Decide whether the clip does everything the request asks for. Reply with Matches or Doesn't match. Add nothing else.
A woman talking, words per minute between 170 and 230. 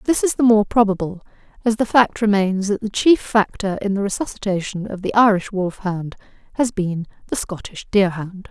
Matches